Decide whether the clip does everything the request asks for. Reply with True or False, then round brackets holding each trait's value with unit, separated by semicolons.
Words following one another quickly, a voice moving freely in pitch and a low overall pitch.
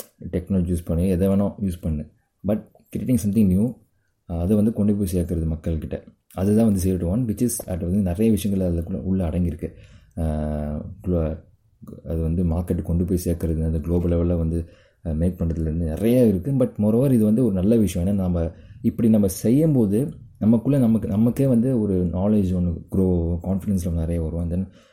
False (165 wpm; 3.8 semitones; 95 Hz)